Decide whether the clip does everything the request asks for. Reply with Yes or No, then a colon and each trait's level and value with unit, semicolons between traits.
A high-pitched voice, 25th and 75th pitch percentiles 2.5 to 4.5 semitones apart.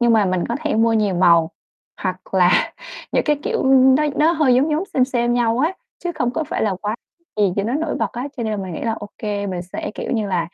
No: high, 230 Hz; average, 5.2 semitones